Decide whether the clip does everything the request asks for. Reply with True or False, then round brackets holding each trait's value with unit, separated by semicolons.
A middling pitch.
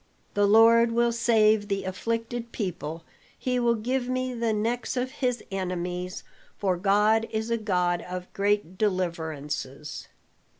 False (210 Hz)